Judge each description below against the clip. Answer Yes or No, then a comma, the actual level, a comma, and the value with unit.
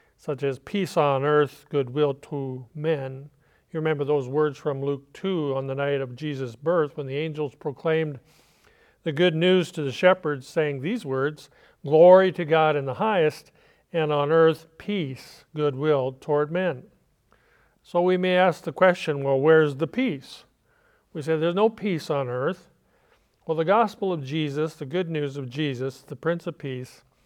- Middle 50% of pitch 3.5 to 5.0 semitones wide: No, average, 3.1 semitones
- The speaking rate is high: No, average, 170 wpm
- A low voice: No, medium, 150 Hz